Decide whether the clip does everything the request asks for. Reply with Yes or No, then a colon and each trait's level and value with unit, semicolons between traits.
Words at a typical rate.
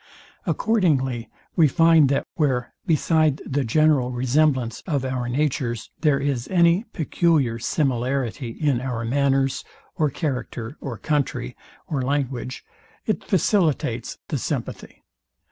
No: slow, 115 wpm